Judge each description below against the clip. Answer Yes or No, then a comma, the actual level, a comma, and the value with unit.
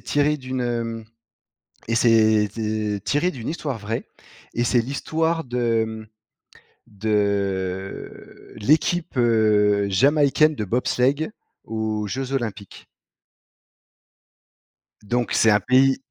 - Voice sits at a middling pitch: No, low, 115 Hz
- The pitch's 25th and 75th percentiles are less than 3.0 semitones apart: No, average, 4.0 semitones